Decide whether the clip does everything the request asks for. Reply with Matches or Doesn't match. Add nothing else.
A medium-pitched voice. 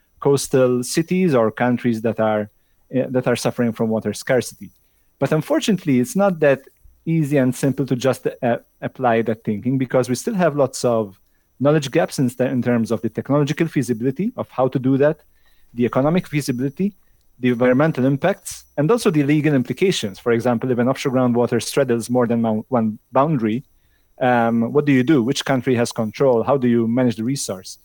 Doesn't match